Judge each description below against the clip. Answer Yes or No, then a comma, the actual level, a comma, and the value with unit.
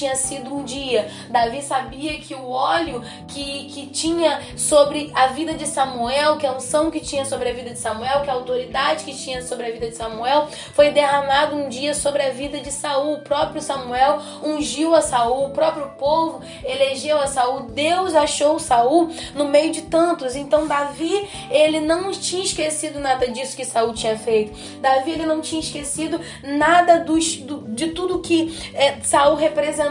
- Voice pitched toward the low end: No, very high, 285 Hz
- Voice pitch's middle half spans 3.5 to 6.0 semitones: No, narrow, 2.6 semitones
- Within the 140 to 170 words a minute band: No, fast, 185 wpm